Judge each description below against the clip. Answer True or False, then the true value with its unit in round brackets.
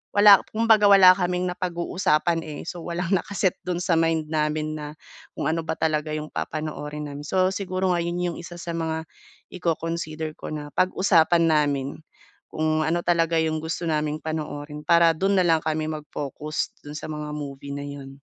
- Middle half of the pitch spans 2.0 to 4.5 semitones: True (2.5 semitones)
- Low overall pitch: False (160 Hz)